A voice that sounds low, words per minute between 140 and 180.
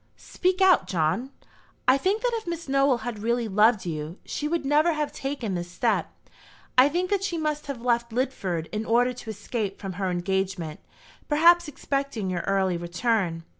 No: high, 235 Hz; average, 175 wpm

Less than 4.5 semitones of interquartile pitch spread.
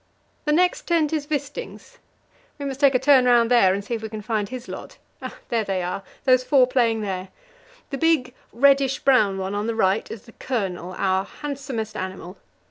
No: wide, 5.4 semitones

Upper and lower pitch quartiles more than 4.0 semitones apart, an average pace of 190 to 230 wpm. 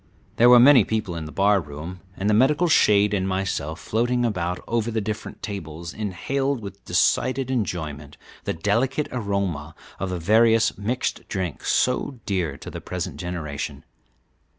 No: average, 5.2 semitones; average, 155 wpm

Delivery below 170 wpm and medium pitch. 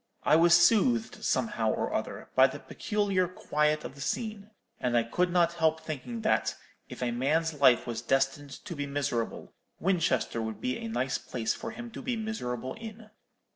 No: average, 180 wpm; medium, 160 Hz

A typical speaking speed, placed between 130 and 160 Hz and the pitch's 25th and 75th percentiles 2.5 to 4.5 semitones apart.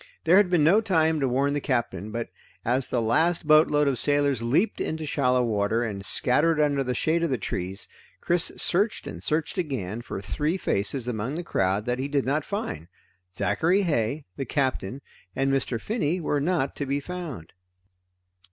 No: average, 180 wpm; medium, 140 Hz; average, 5.3 semitones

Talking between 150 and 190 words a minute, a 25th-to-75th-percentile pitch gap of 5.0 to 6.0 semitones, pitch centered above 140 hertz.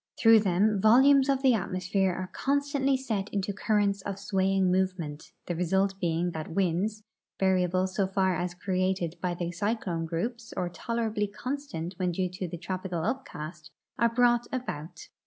No: average, 160 wpm; average, 3.8 semitones; high, 190 Hz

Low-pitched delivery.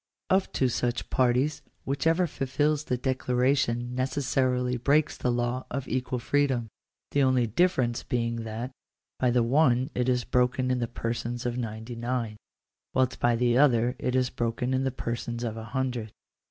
Yes: low, 125 Hz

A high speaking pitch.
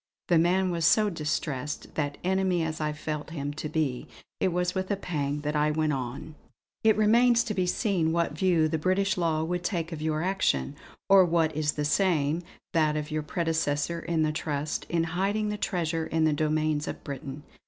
No: medium, 160 Hz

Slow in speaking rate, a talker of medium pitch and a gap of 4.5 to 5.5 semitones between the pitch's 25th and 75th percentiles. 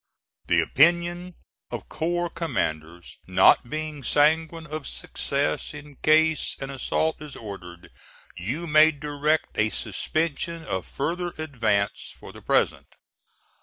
Yes: slow, 120 wpm; medium, 150 Hz; average, 5.2 semitones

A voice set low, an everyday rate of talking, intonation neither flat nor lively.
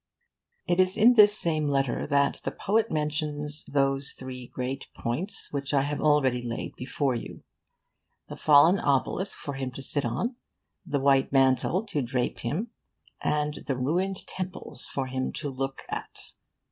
No: medium, 145 Hz; average, 160 wpm; average, 4.2 semitones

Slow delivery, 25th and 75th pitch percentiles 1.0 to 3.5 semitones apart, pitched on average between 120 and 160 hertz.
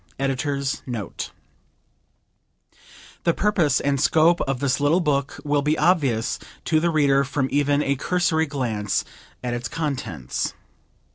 Yes: slow, 130 wpm; average, 2.9 semitones; medium, 140 Hz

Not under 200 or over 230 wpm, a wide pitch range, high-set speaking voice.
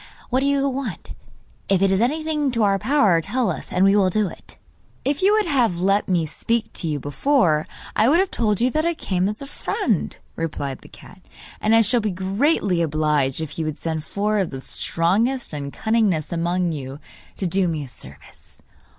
Yes: fast, 205 wpm; wide, 7.0 semitones; high, 195 Hz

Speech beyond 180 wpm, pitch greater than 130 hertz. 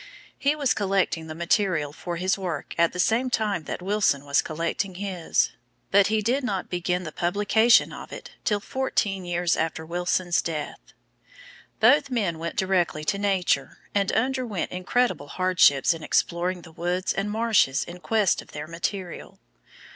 No: average, 160 wpm; medium, 185 Hz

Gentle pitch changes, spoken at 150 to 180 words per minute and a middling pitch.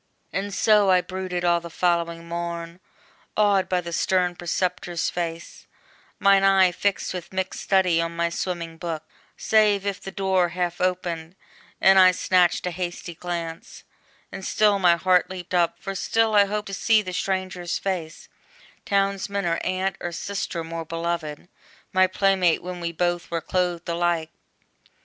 Yes: narrow, 2.1 semitones; average, 160 wpm; medium, 180 Hz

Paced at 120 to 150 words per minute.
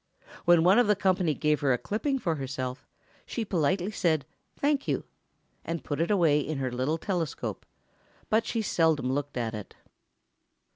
No: average, 165 wpm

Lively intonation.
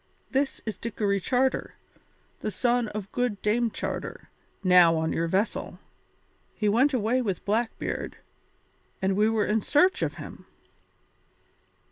No: average, 3.7 semitones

